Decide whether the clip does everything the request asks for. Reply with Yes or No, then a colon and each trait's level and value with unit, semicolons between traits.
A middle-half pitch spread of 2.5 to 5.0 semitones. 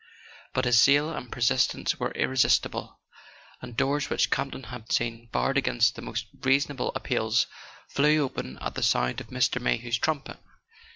Yes: average, 3.1 semitones